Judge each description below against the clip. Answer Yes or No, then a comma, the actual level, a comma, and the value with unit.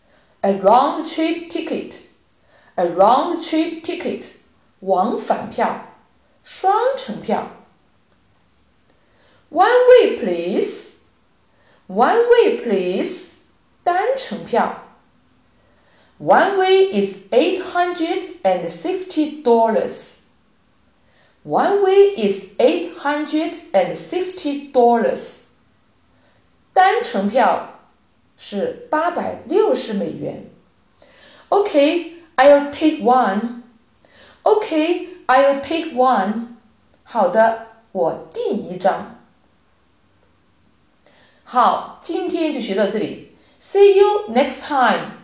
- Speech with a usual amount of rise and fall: No, wide, 7.7 semitones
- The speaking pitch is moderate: No, very high, 320 Hz